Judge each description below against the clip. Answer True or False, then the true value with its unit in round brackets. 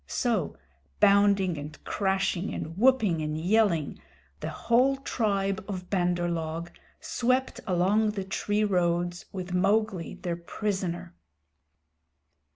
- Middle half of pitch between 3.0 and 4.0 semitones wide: True (3.4 semitones)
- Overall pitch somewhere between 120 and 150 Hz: False (190 Hz)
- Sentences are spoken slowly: True (110 wpm)